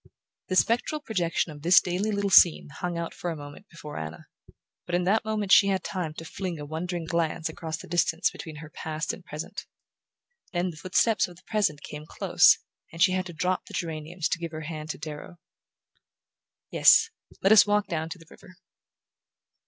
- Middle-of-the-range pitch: Yes, medium, 175 Hz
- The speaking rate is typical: Yes, average, 195 wpm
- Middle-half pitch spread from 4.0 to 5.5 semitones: No, average, 2.9 semitones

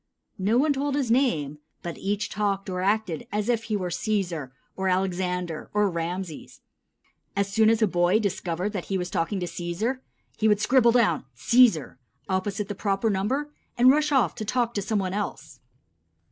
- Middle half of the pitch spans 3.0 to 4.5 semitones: Yes, average, 3.8 semitones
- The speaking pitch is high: Yes, high, 200 Hz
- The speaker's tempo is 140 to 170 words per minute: No, average, 180 wpm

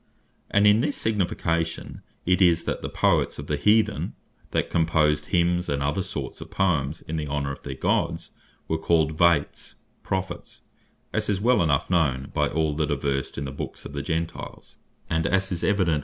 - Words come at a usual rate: Yes, average, 190 wpm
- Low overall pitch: Yes, very low, 80 Hz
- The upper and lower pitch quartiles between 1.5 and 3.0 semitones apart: No, average, 4.0 semitones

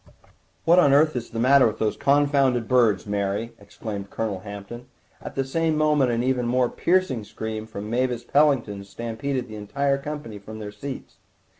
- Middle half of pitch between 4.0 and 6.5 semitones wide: Yes, average, 4.5 semitones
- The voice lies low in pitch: Yes, low, 120 Hz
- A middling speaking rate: Yes, average, 170 wpm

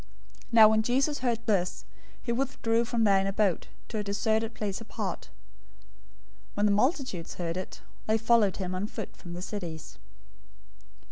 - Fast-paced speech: No, average, 165 wpm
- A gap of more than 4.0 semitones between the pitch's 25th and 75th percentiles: No, average, 3.2 semitones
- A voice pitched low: No, high, 215 Hz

